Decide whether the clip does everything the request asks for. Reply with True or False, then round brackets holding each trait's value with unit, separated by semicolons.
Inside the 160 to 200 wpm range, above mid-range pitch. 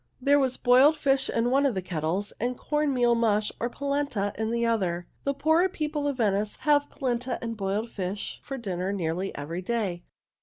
True (195 wpm; 235 Hz)